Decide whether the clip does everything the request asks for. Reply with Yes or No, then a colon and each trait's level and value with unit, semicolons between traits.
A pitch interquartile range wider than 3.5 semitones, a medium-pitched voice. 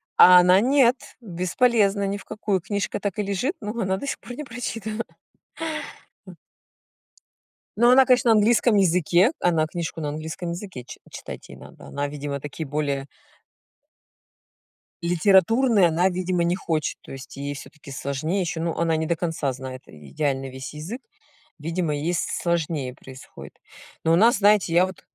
Yes: average, 5.3 semitones; medium, 175 Hz